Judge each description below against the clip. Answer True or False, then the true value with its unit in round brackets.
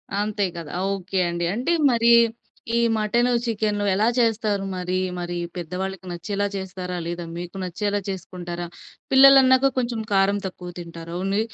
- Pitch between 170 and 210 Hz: True (195 Hz)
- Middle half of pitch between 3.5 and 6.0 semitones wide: True (3.8 semitones)